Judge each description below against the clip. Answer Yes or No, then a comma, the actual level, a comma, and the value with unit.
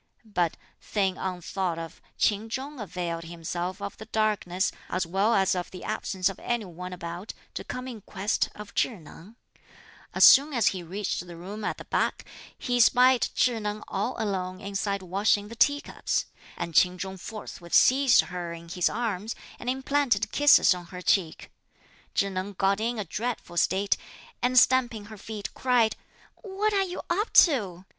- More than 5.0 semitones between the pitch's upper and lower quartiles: No, average, 4.5 semitones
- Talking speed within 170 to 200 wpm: Yes, average, 175 wpm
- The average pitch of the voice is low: No, high, 200 Hz